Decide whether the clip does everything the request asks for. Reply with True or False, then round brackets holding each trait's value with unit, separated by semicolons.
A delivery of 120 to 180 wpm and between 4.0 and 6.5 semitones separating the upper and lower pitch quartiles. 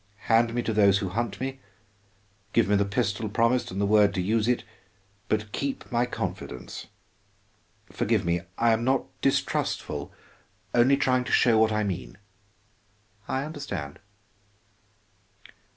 False (140 wpm; 3.4 semitones)